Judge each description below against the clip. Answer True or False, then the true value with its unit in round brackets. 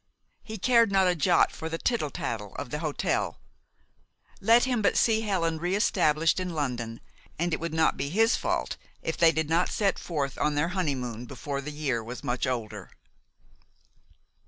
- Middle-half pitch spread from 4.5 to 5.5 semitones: True (5.2 semitones)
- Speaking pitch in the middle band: True (160 Hz)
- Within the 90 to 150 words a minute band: False (180 wpm)